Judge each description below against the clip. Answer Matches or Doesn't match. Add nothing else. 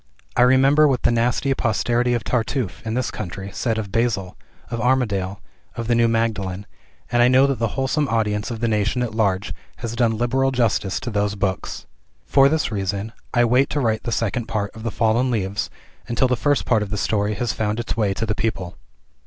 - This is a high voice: Doesn't match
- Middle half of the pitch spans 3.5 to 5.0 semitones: Doesn't match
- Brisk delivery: Matches